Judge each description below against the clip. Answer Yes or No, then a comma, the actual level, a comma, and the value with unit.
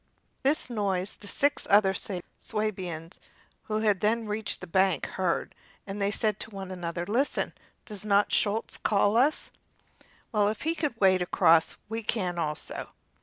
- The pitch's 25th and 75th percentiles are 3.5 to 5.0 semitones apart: No, average, 2.8 semitones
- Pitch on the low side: No, high, 205 Hz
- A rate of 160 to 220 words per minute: No, average, 150 wpm